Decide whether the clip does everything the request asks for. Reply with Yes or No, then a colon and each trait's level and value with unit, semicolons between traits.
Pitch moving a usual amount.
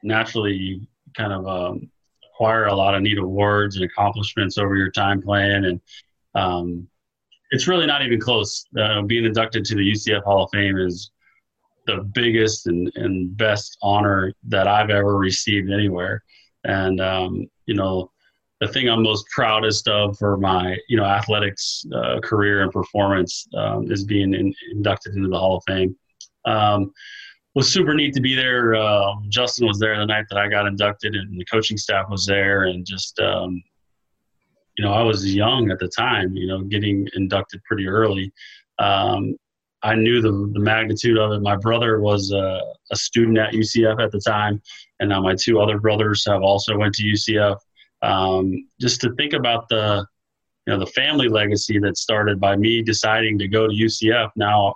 No: narrow, 2.1 semitones